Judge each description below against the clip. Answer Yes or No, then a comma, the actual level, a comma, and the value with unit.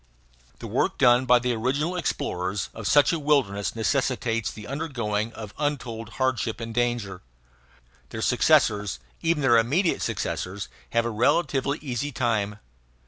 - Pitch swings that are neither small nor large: Yes, average, 4.4 semitones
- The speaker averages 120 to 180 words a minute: Yes, average, 140 wpm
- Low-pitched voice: Yes, low, 120 Hz